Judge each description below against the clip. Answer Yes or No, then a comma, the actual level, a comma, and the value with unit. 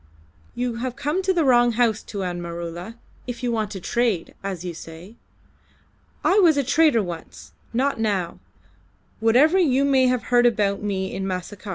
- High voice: Yes, high, 225 Hz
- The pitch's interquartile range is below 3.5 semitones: No, average, 5.3 semitones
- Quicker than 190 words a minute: No, average, 170 wpm